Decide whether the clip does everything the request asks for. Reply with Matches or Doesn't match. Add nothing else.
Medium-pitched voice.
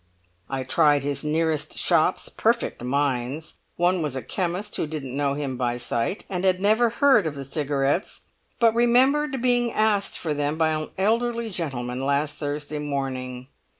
Matches